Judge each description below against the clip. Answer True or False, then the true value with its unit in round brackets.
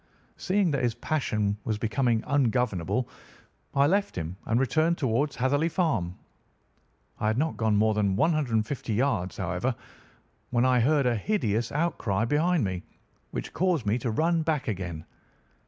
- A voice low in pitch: True (125 Hz)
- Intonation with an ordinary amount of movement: False (6.0 semitones)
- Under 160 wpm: True (150 wpm)